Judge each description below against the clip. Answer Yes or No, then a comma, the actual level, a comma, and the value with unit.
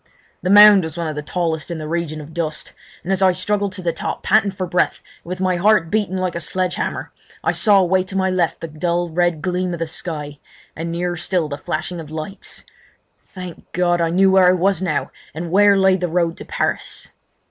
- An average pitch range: No, narrow, 2.3 semitones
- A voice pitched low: No, medium, 175 Hz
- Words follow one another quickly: Yes, fast, 225 wpm